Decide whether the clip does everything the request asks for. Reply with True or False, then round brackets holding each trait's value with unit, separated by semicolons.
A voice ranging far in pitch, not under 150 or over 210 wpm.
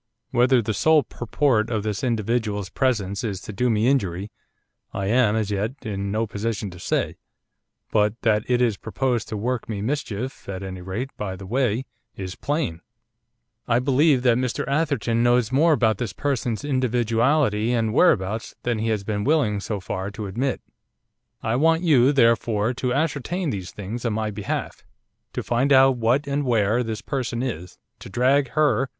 False (4.0 semitones; 175 wpm)